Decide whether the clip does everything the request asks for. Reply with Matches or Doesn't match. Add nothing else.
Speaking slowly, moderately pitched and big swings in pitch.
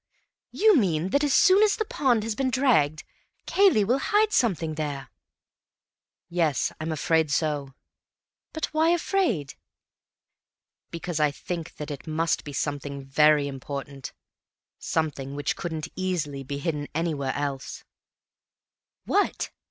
Matches